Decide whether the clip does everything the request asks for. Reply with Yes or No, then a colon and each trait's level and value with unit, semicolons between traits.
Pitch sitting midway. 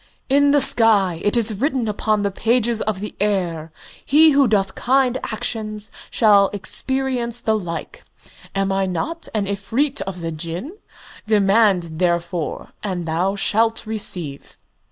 No: high, 210 Hz